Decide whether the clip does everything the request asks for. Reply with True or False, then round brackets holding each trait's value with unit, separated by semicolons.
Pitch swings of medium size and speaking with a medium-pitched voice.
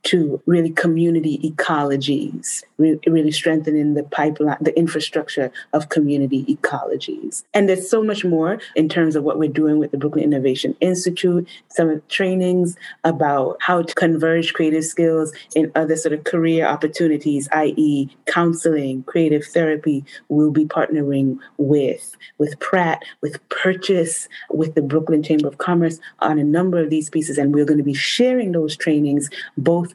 False (2.2 semitones; 155 Hz)